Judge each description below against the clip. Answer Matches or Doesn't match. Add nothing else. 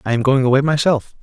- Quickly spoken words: Matches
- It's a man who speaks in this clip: Matches